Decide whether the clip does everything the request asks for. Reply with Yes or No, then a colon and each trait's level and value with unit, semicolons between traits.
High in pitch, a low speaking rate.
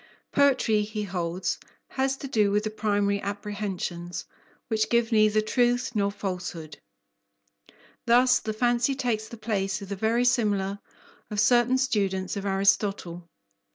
Yes: high, 210 Hz; slow, 130 wpm